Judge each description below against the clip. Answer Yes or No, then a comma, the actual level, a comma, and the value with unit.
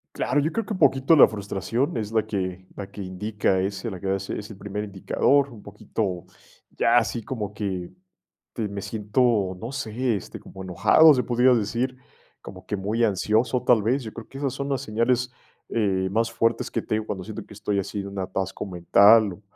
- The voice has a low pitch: Yes, low, 105 Hz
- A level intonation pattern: No, average, 3.6 semitones